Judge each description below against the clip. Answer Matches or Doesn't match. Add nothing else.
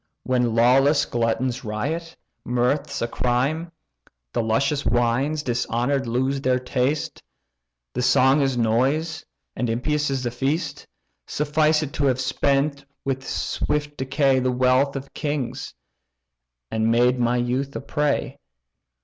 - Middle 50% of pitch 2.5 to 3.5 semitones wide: Matches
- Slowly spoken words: Matches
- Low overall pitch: Matches